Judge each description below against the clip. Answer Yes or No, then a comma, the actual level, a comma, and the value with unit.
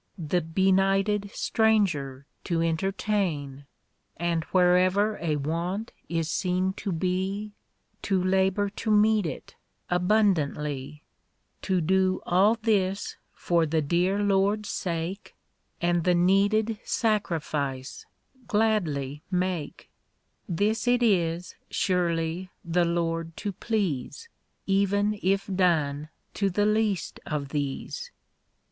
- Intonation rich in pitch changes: No, average, 3.6 semitones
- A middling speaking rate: No, slow, 105 wpm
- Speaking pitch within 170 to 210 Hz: Yes, medium, 185 Hz